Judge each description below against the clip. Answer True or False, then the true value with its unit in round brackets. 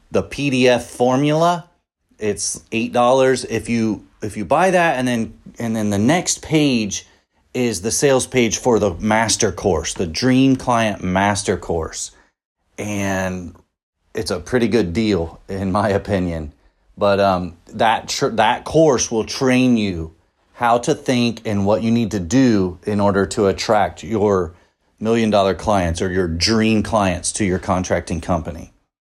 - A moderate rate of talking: True (155 wpm)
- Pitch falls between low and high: False (105 Hz)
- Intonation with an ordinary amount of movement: True (4.2 semitones)